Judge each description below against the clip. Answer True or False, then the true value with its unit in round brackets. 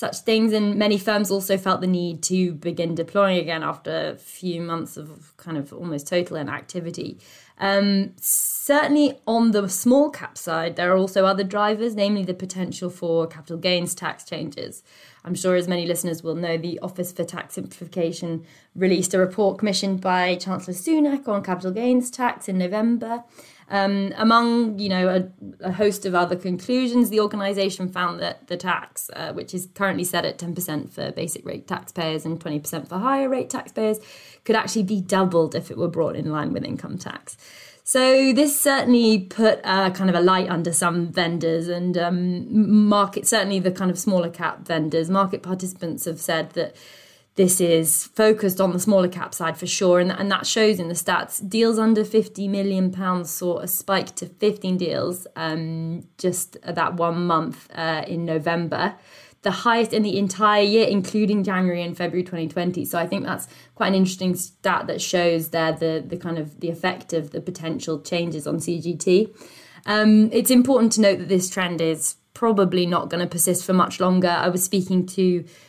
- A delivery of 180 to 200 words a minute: True (185 wpm)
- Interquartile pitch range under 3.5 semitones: True (3.1 semitones)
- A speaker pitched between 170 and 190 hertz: True (185 Hz)